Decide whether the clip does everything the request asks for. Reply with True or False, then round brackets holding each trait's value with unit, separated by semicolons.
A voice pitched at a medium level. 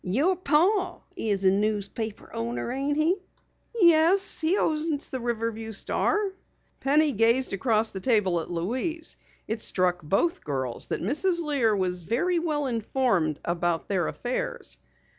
False (235 Hz)